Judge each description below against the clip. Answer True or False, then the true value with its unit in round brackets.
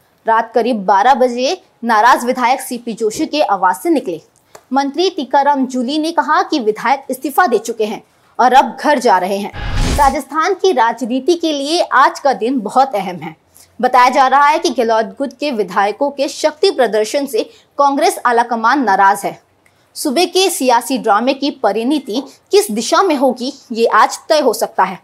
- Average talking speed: True (175 wpm)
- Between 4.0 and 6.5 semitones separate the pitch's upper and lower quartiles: True (5.0 semitones)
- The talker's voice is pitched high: True (260 Hz)